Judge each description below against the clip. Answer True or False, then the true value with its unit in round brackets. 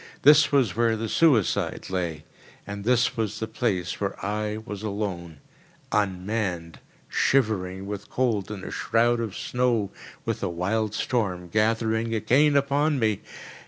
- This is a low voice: True (110 Hz)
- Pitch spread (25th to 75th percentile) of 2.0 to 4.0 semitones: True (3.3 semitones)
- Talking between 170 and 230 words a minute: False (135 wpm)